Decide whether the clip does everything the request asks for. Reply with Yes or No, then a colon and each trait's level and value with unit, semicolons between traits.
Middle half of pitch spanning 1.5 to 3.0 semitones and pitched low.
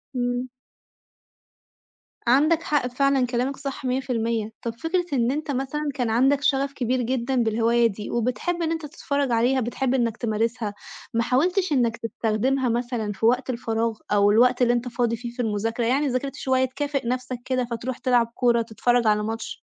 No: narrow, 2.6 semitones; high, 245 Hz